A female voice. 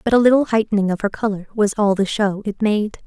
Yes: female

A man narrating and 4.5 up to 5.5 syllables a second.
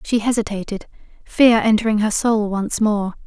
No: female; 4.7 syllables/s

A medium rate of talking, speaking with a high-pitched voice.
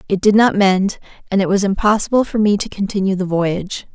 No: fast, 215 wpm; high, 195 Hz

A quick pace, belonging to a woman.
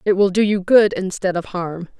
Yes: fast, 240 wpm; female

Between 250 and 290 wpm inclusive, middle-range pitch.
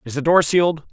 Yes: fast, 260 wpm; medium, 150 Hz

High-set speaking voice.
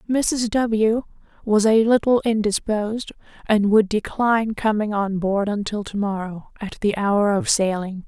Yes: high, 210 Hz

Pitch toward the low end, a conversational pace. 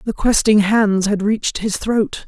No: high, 210 Hz; average, 185 wpm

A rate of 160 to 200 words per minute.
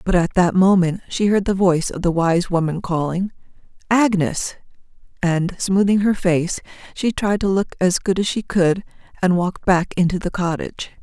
Yes: average, 180 wpm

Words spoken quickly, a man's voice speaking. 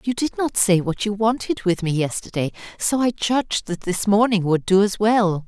No: fast, 220 wpm; female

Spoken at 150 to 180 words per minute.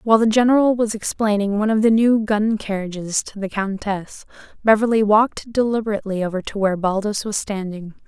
Yes: average, 170 wpm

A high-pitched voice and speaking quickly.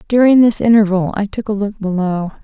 No: high, 205 Hz; average, 195 wpm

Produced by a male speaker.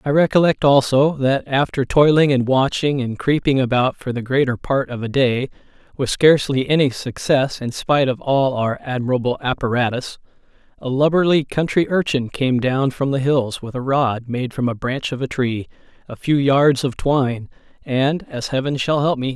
Yes: male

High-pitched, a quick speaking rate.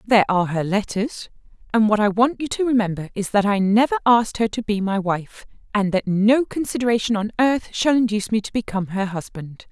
Yes: high, 215 Hz; fast, 210 wpm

